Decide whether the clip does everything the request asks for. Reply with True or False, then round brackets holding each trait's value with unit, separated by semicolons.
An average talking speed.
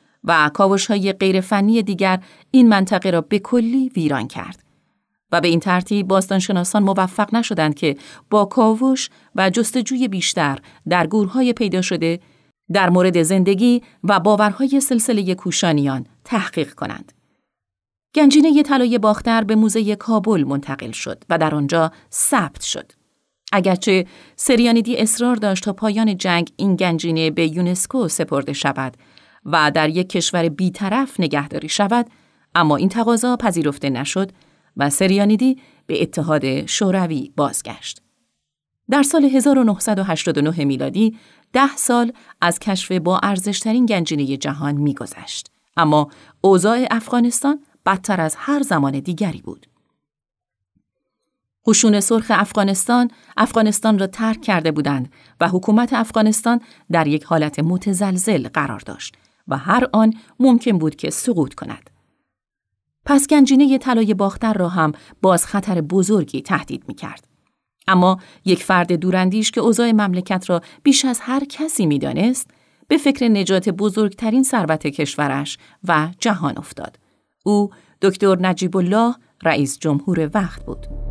True (130 wpm)